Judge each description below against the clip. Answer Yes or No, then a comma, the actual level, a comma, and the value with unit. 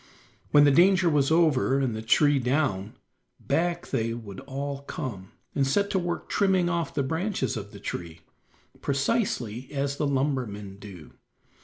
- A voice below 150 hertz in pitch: Yes, medium, 140 Hz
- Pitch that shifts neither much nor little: No, wide, 6.3 semitones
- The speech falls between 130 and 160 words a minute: Yes, average, 155 wpm